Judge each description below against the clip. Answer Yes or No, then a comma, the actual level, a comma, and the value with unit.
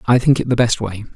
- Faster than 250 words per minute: Yes, fast, 315 wpm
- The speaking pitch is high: No, low, 115 Hz